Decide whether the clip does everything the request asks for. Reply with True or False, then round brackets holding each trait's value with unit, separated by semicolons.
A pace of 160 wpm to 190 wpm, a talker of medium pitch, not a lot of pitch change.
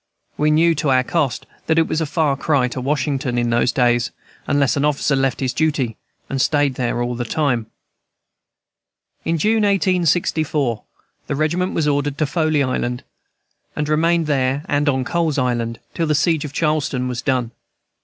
False (175 wpm; 145 Hz; 3.7 semitones)